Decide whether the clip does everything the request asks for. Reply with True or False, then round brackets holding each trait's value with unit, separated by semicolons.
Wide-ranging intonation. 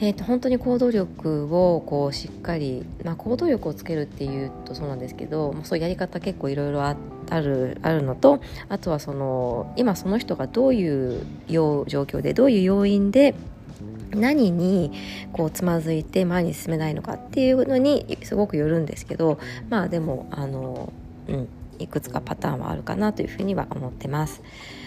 True (6.1 semitones)